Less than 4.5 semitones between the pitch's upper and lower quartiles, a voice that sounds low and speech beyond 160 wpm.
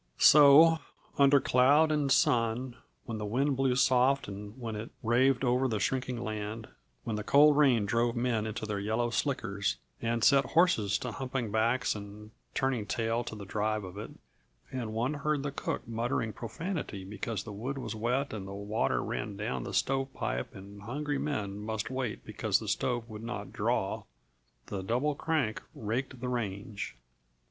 Yes: average, 4.0 semitones; low, 115 Hz; average, 170 wpm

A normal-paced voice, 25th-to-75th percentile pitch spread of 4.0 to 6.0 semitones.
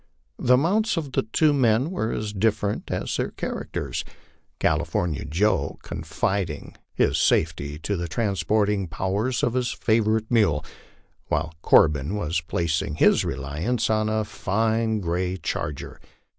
No: slow, 130 wpm; average, 5.1 semitones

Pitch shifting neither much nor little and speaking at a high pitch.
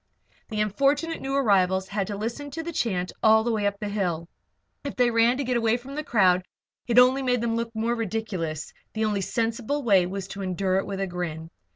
Yes: average, 4.1 semitones; high, 220 Hz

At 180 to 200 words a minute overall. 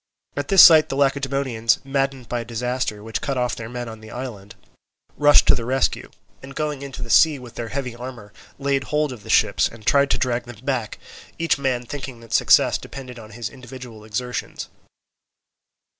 Yes: average, 190 wpm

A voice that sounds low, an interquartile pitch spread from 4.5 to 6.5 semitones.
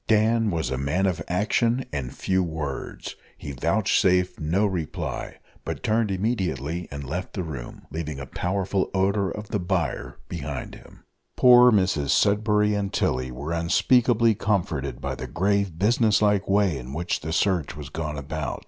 Yes: very low, 90 Hz; average, 5.2 semitones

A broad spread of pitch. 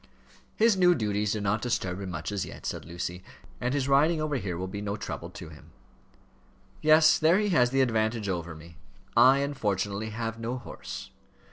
Yes: wide, 6.1 semitones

